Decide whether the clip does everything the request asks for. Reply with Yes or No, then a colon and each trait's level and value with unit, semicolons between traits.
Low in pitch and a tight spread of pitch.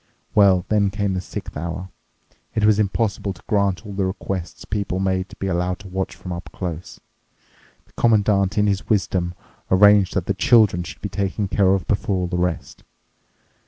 Yes: very low, 95 Hz; narrow, 1.9 semitones